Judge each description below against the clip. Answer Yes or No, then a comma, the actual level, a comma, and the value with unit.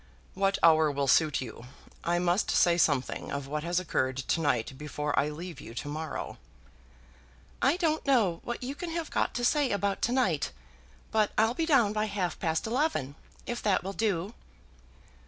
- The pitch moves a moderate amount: No, wide, 7.8 semitones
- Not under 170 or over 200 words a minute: Yes, average, 180 wpm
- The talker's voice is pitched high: No, medium, 180 Hz